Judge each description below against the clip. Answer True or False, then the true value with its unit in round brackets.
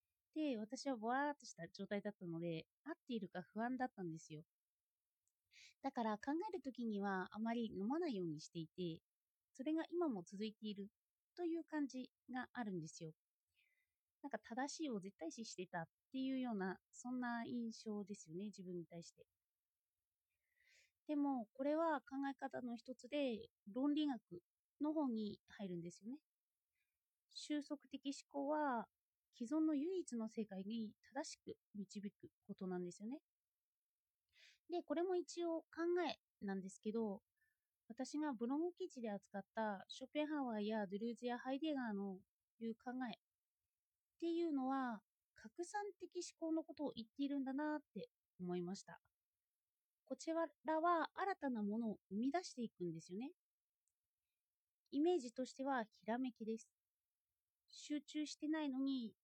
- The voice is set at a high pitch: True (245 Hz)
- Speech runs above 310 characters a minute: False (295 characters per minute)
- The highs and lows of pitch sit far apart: True (6.5 semitones)